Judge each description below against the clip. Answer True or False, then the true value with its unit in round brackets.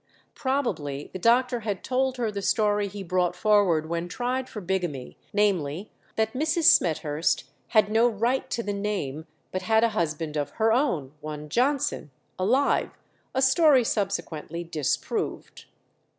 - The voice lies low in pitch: False (205 Hz)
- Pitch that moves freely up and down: True (6.4 semitones)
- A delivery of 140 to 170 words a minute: True (145 wpm)